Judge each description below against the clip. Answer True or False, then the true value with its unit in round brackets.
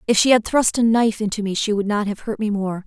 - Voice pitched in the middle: False (215 Hz)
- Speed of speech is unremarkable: False (315 wpm)